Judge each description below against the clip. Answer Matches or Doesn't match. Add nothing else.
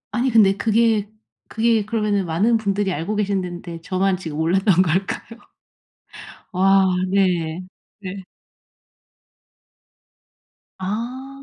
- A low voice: Doesn't match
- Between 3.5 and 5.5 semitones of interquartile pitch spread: Doesn't match